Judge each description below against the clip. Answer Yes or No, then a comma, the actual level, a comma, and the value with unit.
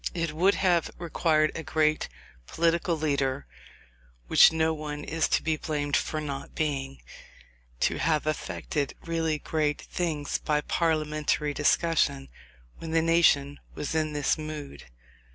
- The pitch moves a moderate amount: No, narrow, 1.8 semitones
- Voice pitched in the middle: Yes, medium, 155 Hz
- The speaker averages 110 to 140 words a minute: Yes, slow, 135 wpm